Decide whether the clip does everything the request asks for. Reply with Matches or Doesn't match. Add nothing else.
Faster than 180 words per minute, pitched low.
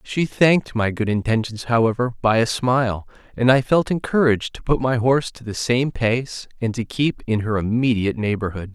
Matches